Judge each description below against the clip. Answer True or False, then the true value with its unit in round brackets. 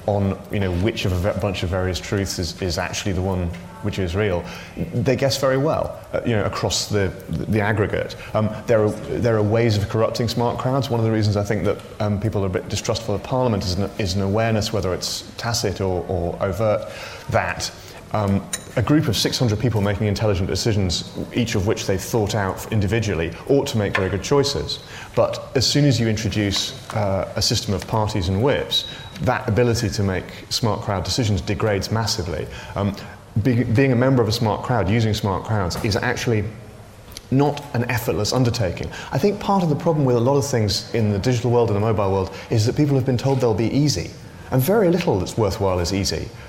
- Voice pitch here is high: False (105 Hz)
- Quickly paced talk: True (215 wpm)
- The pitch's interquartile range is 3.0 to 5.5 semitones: True (3.5 semitones)